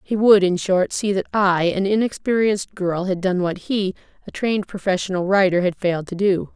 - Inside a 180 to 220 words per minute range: Yes, average, 200 wpm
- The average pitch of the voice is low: No, high, 190 Hz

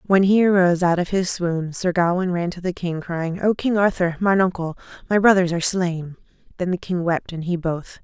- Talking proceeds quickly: Yes, fast, 225 wpm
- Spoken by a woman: Yes, female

